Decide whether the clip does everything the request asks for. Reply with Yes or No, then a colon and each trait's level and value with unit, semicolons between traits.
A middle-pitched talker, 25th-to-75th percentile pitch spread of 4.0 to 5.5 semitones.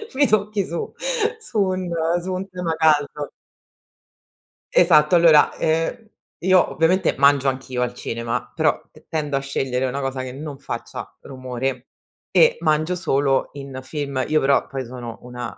Yes: medium, 145 Hz; average, 4.8 semitones